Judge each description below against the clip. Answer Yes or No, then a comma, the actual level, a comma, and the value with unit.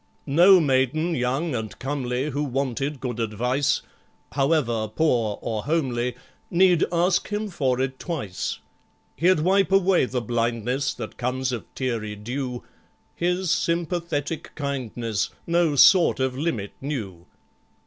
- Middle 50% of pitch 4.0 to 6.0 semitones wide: Yes, wide, 5.5 semitones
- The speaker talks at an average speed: No, slow, 125 wpm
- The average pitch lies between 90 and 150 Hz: Yes, low, 135 Hz